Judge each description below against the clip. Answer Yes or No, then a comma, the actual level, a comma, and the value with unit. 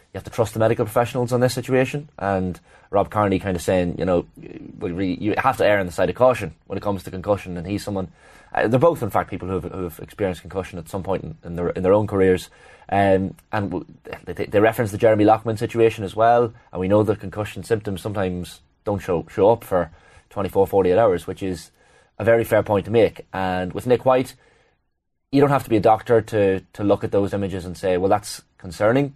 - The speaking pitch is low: Yes, low, 100 Hz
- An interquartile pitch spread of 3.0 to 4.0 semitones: Yes, average, 3.6 semitones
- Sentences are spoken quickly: Yes, fast, 230 wpm